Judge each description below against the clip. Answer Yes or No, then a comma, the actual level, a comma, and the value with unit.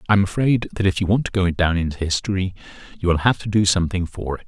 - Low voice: Yes, very low, 95 Hz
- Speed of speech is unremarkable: No, fast, 255 wpm